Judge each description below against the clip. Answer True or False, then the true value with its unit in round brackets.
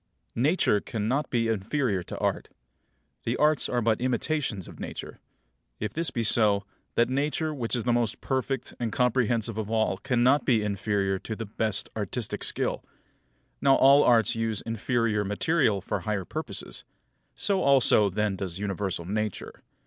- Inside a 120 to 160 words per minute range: True (155 wpm)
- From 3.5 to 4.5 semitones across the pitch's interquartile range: True (3.8 semitones)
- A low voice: True (115 Hz)